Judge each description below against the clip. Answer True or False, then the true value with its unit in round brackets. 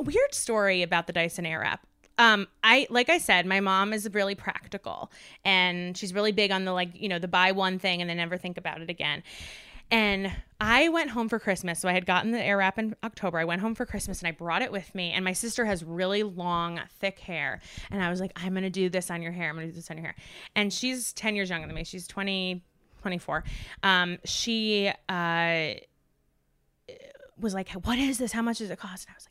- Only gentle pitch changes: False (3.6 semitones)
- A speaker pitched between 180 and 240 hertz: True (190 Hz)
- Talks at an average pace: False (235 wpm)